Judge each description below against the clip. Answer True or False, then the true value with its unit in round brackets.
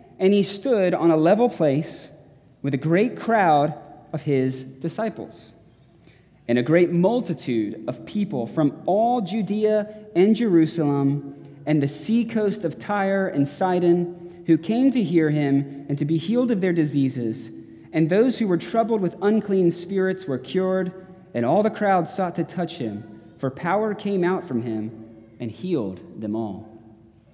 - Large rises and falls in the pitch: True (5.8 semitones)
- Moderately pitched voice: True (170 Hz)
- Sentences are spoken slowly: False (160 wpm)